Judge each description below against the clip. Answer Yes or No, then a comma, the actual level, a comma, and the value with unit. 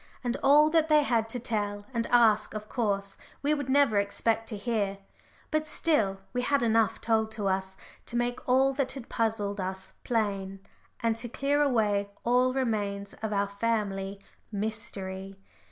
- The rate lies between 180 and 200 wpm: No, average, 165 wpm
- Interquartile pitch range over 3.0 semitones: Yes, average, 3.8 semitones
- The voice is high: Yes, high, 225 Hz